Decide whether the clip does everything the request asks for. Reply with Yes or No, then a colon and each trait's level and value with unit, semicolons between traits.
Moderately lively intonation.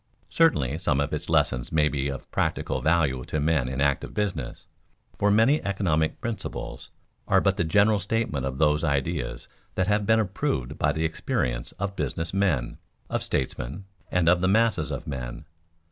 No: wide, 6.3 semitones